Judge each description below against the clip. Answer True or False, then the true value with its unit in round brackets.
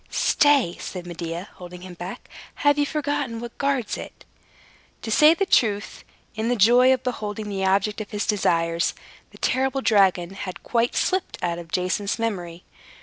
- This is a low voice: False (210 Hz)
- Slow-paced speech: False (165 wpm)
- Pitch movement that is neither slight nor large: False (5.7 semitones)